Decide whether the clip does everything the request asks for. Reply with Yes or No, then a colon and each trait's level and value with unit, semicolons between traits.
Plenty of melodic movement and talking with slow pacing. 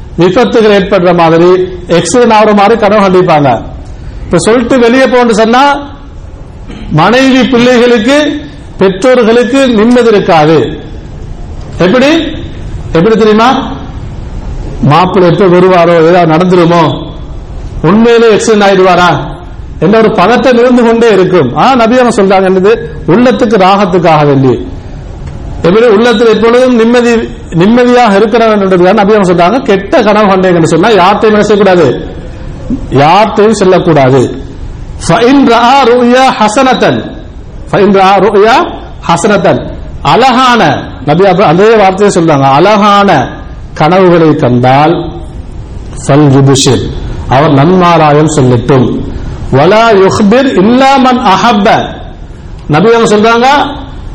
Yes: wide, 5.8 semitones; slow, 95 wpm